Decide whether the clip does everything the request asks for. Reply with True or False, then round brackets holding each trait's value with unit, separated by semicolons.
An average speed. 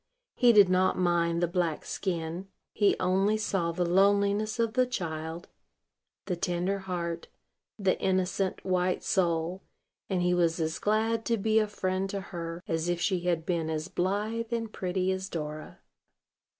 True (160 wpm)